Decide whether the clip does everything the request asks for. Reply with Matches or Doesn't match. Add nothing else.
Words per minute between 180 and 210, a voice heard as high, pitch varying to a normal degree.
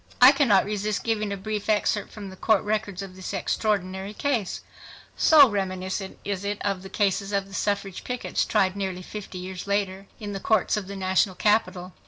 Doesn't match